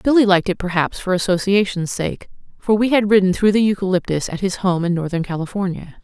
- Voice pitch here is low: No, high, 190 Hz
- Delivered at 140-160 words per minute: No, average, 200 wpm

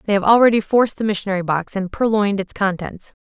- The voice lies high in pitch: Yes, high, 200 Hz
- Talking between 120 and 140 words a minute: No, fast, 205 wpm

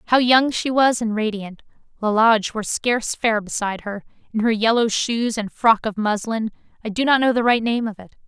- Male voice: No, female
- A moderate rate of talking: No, fast, 210 wpm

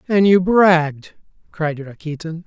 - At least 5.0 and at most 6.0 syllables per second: No, 4.1 syllables/s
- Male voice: Yes, male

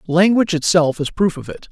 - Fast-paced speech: Yes, fast, 210 wpm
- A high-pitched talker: No, medium, 170 Hz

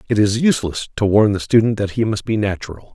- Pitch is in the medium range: No, low, 105 Hz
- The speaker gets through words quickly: Yes, fast, 245 wpm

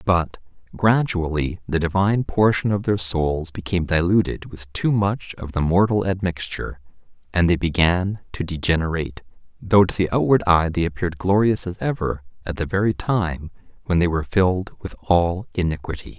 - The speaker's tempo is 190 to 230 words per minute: No, average, 160 wpm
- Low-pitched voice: Yes, very low, 90 Hz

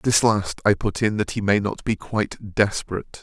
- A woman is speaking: No, male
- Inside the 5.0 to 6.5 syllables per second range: Yes, 5.1 syllables/s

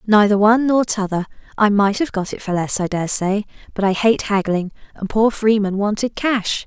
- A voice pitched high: Yes, high, 210 Hz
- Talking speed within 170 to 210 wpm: Yes, fast, 205 wpm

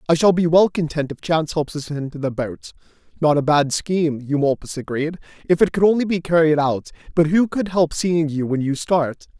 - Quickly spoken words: Yes, fast, 215 wpm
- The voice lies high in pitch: No, medium, 160 Hz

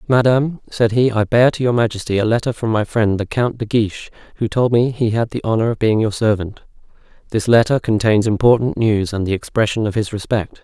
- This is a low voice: Yes, low, 110 Hz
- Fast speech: Yes, fast, 220 wpm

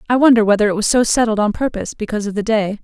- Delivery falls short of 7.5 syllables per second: No, 7.6 syllables/s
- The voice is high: Yes, high, 215 Hz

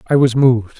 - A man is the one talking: Yes, male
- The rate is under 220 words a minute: No, fast, 225 wpm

